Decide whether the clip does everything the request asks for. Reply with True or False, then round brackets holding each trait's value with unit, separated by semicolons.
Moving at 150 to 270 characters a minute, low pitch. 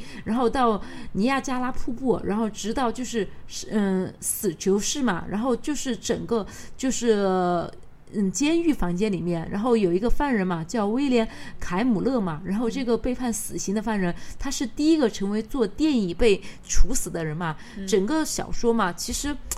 False (255 characters per minute; 225 Hz)